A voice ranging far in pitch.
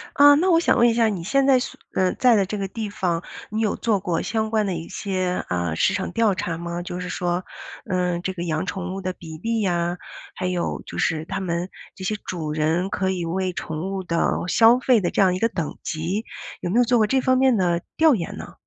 No: average, 4.4 semitones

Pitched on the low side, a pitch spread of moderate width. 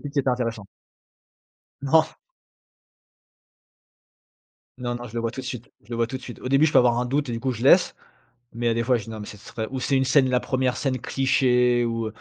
No: low, 125 Hz; narrow, 2.2 semitones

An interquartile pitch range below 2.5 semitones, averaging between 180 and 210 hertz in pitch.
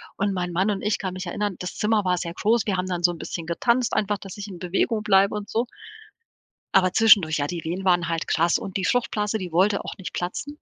No: average, 2.9 semitones; high, 190 Hz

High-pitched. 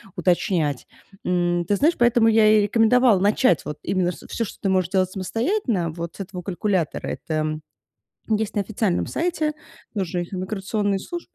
Yes: high, 195 Hz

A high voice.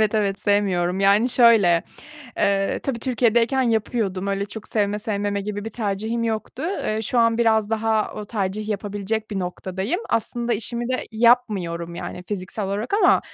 Yes: high, 215 Hz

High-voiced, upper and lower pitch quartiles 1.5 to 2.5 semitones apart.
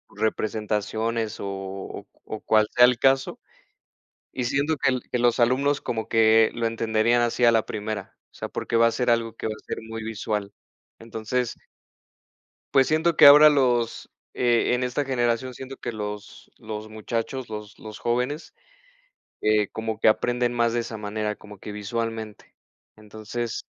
No: low, 115 Hz; narrow, 2.2 semitones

